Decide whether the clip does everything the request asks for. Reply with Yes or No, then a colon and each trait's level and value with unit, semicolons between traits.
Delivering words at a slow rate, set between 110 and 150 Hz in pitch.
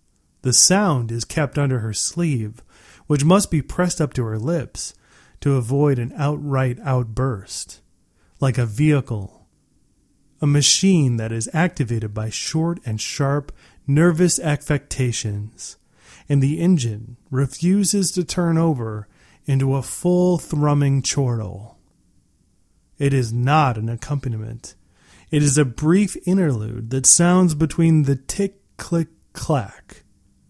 Yes: slow, 125 wpm; low, 135 Hz